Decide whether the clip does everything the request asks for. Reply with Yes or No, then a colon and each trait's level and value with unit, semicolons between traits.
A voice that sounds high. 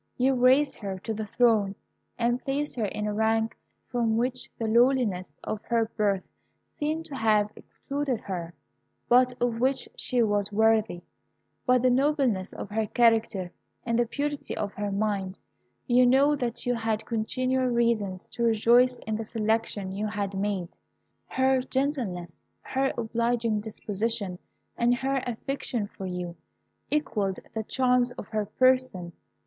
Yes: high, 230 Hz